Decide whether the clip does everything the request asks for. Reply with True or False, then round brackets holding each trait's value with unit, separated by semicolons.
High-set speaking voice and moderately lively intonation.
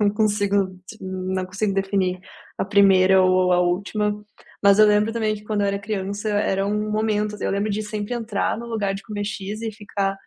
False (205 Hz; 1.6 semitones)